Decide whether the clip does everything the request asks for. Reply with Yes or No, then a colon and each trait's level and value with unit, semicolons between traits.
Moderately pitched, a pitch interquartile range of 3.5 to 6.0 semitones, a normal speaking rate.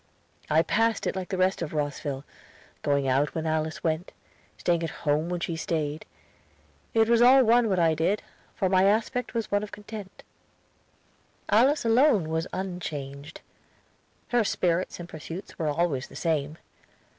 Yes: medium, 175 Hz; average, 5.1 semitones; average, 155 wpm